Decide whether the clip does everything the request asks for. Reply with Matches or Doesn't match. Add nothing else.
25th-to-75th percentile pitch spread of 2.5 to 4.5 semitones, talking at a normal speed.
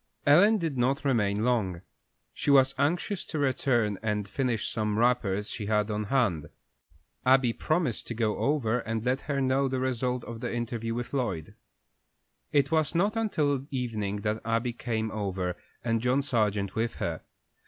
Matches